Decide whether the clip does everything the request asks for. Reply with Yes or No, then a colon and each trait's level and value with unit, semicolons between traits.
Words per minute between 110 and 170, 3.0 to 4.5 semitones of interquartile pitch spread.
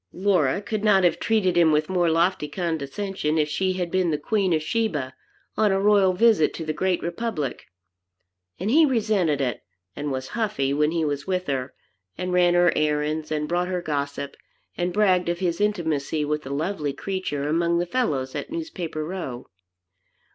No: average, 180 wpm; average, 4.2 semitones